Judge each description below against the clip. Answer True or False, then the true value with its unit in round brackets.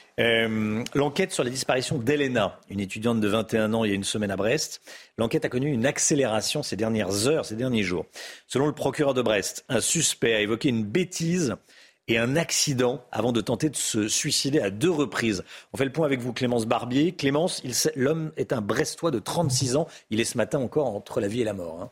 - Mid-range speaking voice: False (125 Hz)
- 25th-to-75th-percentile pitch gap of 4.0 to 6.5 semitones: True (5.2 semitones)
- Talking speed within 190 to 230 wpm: True (220 wpm)